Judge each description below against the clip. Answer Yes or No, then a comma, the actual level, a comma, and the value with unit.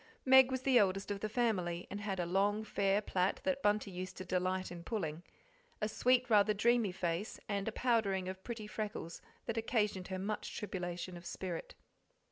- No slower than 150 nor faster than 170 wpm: No, average, 185 wpm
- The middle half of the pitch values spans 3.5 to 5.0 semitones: No, average, 3.0 semitones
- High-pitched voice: Yes, high, 200 Hz